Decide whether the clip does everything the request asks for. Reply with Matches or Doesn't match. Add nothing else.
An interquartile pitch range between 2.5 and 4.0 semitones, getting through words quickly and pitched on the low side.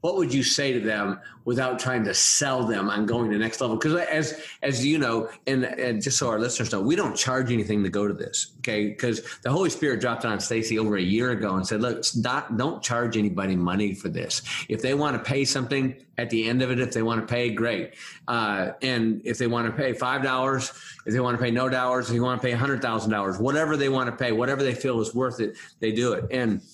Matches